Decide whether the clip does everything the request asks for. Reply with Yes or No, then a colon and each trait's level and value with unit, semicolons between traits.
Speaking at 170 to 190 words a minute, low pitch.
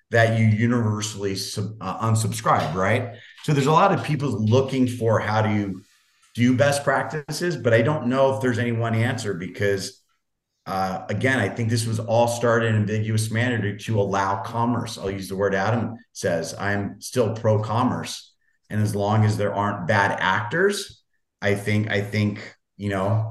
Yes: average, 175 wpm; low, 110 Hz